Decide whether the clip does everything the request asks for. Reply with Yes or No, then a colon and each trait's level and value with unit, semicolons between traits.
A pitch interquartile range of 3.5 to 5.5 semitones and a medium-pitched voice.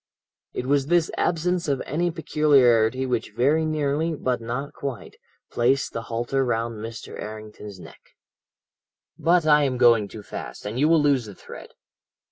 No: average, 4.8 semitones; low, 130 Hz